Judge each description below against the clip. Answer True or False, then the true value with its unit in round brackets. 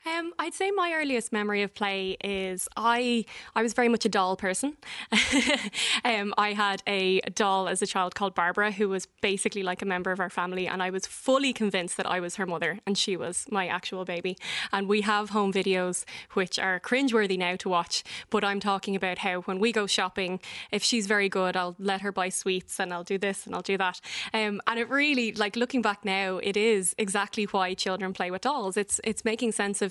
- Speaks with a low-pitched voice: False (200 Hz)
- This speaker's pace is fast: True (220 wpm)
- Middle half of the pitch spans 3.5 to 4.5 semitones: False (2.7 semitones)